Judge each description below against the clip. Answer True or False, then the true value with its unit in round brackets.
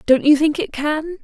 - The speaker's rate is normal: False (245 wpm)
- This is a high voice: True (305 Hz)